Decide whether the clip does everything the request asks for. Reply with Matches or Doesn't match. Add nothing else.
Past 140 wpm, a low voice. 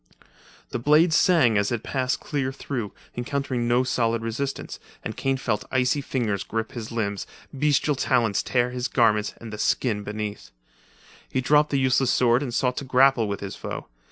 Matches